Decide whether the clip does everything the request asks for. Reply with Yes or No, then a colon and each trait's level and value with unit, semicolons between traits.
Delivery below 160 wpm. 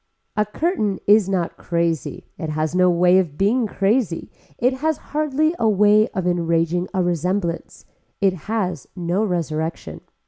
Yes: average, 145 wpm